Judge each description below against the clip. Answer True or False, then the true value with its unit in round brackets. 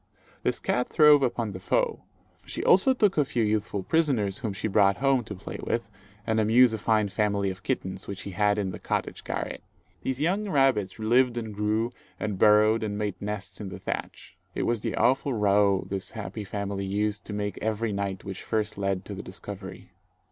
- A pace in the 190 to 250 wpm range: True (200 wpm)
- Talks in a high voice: False (105 Hz)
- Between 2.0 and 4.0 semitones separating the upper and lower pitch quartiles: True (2.9 semitones)